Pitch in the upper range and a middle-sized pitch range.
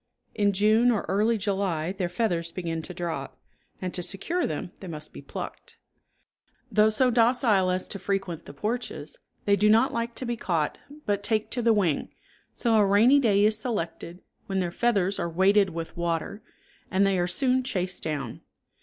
Yes: high, 200 Hz; average, 4.2 semitones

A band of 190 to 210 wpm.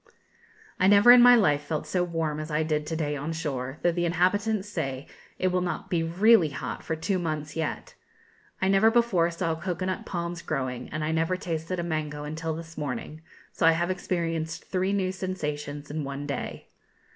Yes: average, 195 wpm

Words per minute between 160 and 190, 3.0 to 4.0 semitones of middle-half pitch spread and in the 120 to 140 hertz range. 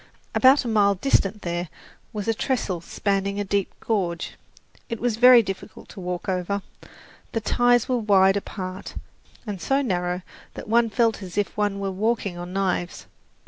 No: average, 165 wpm; average, 3.5 semitones; high, 200 Hz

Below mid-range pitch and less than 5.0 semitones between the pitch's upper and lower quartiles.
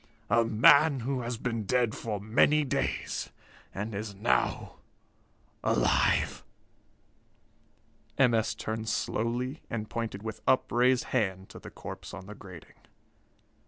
Yes: low, 115 Hz; average, 2.8 semitones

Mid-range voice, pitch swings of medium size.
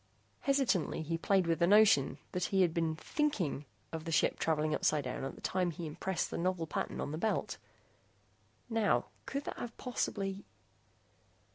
Yes: medium, 175 Hz; average, 4.2 semitones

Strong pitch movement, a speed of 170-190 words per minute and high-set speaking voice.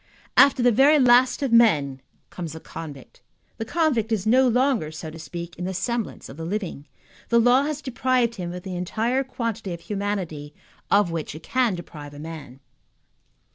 Yes: wide, 7.0 semitones; average, 180 wpm; high, 205 Hz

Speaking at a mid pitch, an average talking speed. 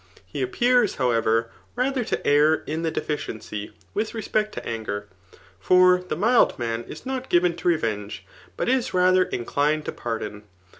Yes: medium, 160 Hz; average, 160 wpm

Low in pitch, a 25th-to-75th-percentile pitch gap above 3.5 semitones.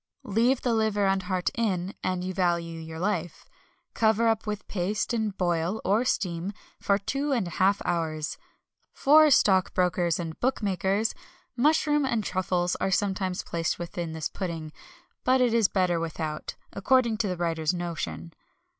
No: high, 190 Hz; average, 4.2 semitones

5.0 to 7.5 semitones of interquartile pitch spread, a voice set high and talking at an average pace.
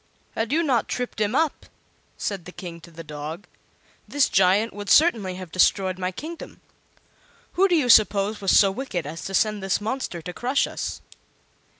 Yes: average, 5.3 semitones; high, 200 Hz; average, 180 wpm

